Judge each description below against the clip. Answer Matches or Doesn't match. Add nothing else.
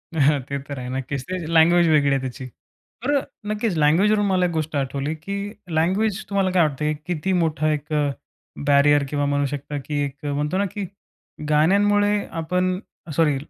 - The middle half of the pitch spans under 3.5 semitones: Doesn't match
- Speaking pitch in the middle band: Matches